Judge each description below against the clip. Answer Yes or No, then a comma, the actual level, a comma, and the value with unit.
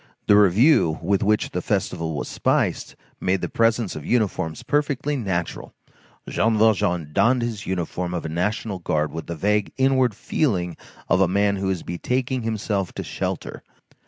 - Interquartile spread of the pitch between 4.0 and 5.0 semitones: Yes, average, 4.7 semitones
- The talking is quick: No, average, 160 wpm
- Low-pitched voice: Yes, low, 100 Hz